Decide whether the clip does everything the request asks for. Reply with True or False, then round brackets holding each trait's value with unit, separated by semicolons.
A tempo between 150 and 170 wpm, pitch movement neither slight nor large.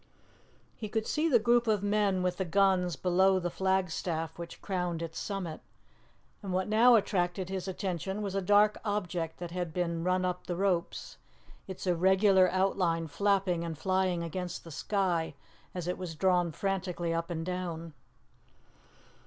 False (160 wpm; 2.3 semitones)